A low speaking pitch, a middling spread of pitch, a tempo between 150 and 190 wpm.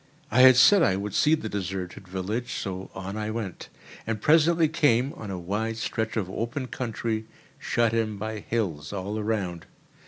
Yes: low, 110 Hz; average, 3.5 semitones; average, 175 wpm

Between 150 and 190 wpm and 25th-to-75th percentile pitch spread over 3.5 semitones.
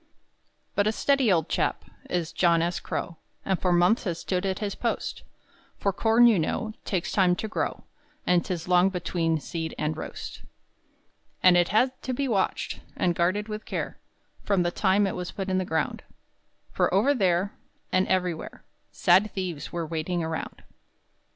No: average, 170 wpm; average, 3.0 semitones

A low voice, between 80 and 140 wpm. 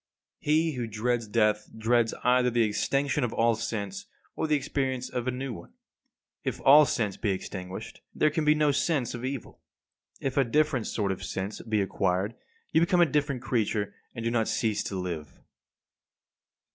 No: low, 120 Hz; average, 180 wpm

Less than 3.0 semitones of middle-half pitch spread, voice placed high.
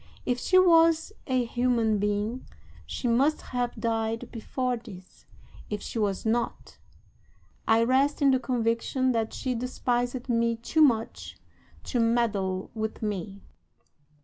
Yes: narrow, 2.5 semitones; high, 235 Hz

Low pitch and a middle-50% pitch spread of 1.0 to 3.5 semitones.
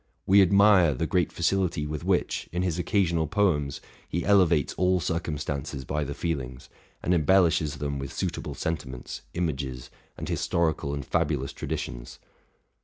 No: very low, 80 Hz; average, 3.9 semitones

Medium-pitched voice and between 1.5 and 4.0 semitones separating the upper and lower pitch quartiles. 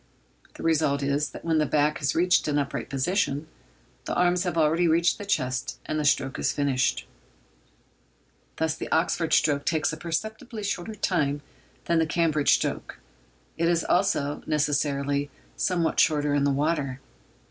Yes: medium, 155 Hz; average, 2.9 semitones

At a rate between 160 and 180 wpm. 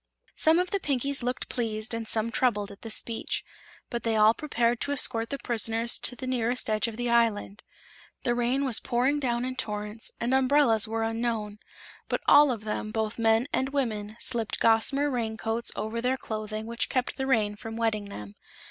No: average, 190 wpm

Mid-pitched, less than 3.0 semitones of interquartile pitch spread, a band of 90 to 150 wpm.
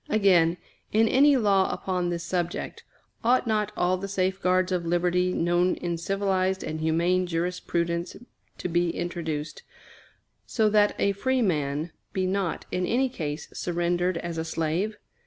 Yes: medium, 180 Hz; narrow, 2.5 semitones; average, 145 wpm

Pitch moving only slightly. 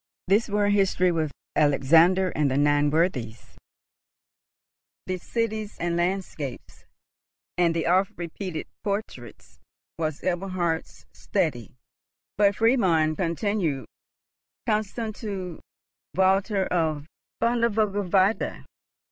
No: average, 4.1 semitones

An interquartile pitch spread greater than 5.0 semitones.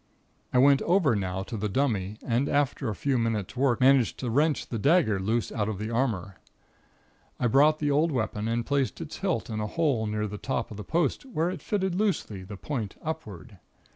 Yes: wide, 5.6 semitones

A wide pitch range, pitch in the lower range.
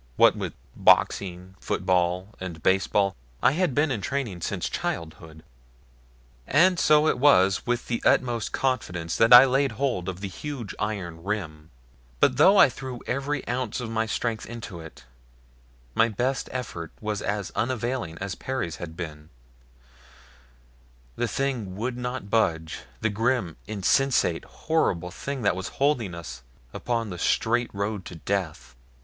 Yes: wide, 6.0 semitones; low, 110 Hz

